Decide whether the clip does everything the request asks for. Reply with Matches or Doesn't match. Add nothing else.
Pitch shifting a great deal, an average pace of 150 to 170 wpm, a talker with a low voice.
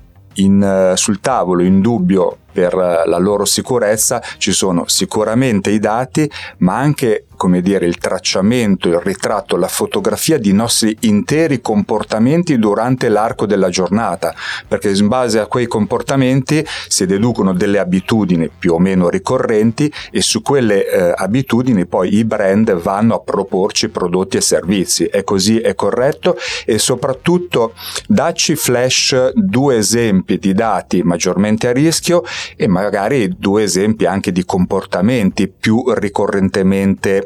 Doesn't match